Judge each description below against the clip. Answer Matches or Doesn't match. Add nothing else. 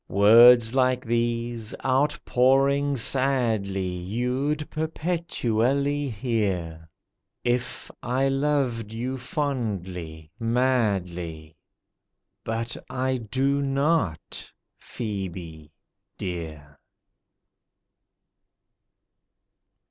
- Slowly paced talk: Matches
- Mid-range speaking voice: Doesn't match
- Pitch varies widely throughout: Matches